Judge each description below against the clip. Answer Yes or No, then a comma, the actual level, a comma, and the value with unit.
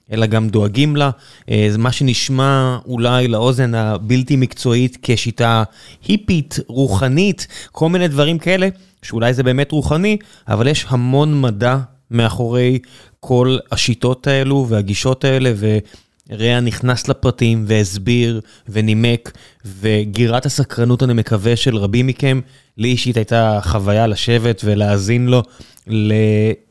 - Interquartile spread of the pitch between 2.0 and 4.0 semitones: Yes, average, 3.3 semitones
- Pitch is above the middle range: No, low, 120 Hz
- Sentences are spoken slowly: No, average, 115 wpm